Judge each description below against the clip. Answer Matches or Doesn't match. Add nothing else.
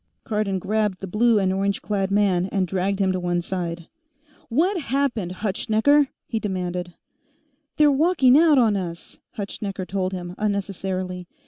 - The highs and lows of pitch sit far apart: Doesn't match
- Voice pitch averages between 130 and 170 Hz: Doesn't match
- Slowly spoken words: Doesn't match